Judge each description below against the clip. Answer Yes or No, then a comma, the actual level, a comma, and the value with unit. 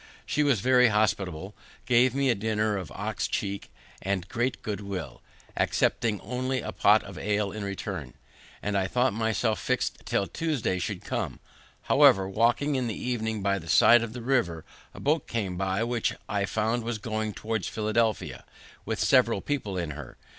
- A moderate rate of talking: Yes, average, 175 wpm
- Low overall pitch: Yes, low, 110 Hz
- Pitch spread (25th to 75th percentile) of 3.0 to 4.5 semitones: Yes, average, 3.4 semitones